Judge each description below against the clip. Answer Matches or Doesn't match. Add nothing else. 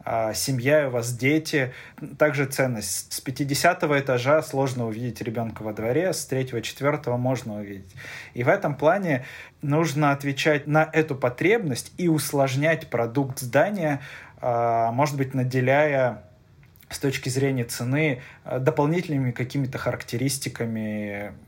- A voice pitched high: Doesn't match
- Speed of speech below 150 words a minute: Matches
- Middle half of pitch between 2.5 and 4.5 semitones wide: Matches